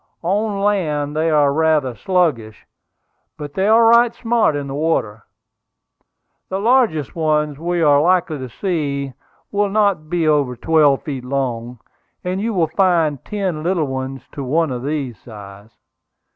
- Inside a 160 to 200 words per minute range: No, average, 150 wpm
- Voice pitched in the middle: Yes, medium, 155 Hz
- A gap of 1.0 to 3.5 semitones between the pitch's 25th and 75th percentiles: No, average, 5.2 semitones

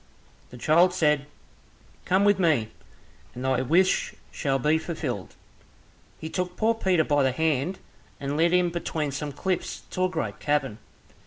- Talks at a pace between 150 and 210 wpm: Yes, average, 155 wpm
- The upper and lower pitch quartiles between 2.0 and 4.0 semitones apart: No, average, 4.7 semitones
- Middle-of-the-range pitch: Yes, medium, 155 Hz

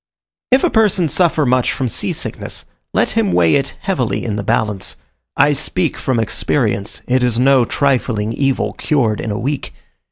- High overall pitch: No, low, 125 Hz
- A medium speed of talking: Yes, average, 170 wpm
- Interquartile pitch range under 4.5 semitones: No, average, 5.0 semitones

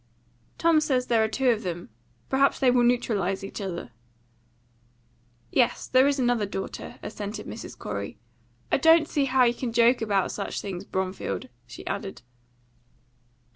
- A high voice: Yes, high, 230 Hz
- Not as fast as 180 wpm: Yes, average, 150 wpm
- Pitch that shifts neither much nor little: Yes, average, 4.7 semitones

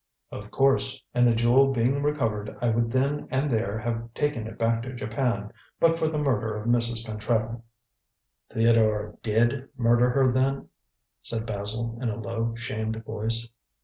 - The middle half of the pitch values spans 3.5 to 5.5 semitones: No, narrow, 2.6 semitones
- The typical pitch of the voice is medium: No, low, 115 Hz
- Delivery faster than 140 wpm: Yes, average, 160 wpm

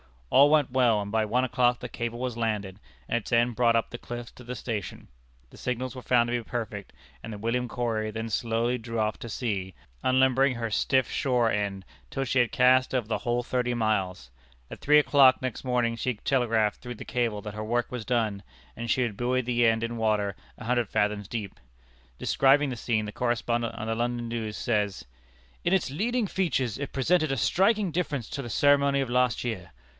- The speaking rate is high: Yes, fast, 210 wpm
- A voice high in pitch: No, low, 120 Hz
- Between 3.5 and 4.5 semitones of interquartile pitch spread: No, narrow, 2.6 semitones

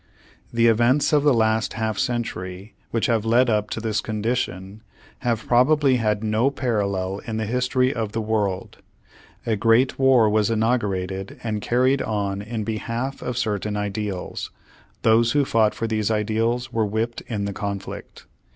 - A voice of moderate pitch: No, low, 110 Hz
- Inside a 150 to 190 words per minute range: Yes, average, 160 wpm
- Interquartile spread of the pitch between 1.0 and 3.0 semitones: Yes, narrow, 2.4 semitones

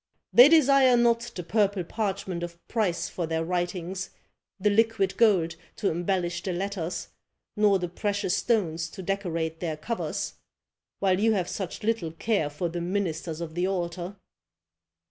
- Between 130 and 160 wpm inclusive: Yes, average, 150 wpm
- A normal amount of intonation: Yes, average, 3.4 semitones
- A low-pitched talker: No, medium, 185 Hz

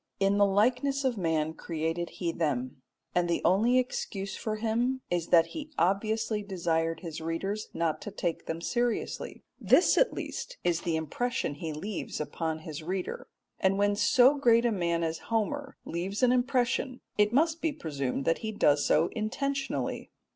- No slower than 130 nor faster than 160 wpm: No, average, 170 wpm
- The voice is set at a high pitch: Yes, high, 195 Hz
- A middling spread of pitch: No, wide, 6.5 semitones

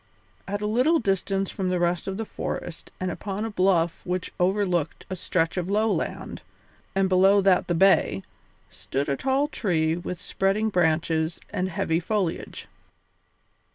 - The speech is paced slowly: No, average, 155 wpm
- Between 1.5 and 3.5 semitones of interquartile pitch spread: Yes, average, 2.7 semitones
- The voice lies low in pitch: No, medium, 185 Hz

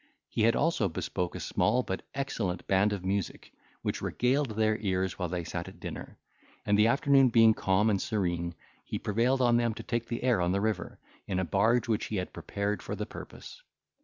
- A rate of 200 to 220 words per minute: Yes, fast, 205 wpm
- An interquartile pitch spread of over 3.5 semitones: Yes, average, 3.9 semitones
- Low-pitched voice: Yes, low, 105 Hz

